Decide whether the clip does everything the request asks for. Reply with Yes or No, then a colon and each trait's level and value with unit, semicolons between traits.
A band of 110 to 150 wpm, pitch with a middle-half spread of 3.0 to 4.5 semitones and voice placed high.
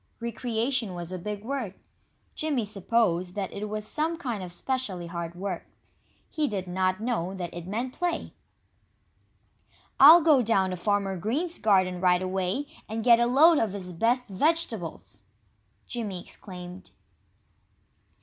No: average, 140 wpm; average, 5.2 semitones; high, 210 Hz